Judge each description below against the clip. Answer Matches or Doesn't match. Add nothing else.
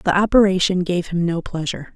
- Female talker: Matches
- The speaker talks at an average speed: Matches